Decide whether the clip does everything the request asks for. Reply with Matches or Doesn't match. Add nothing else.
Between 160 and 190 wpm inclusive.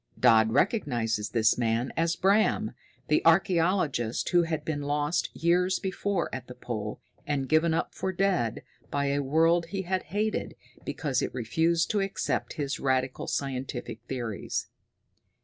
Doesn't match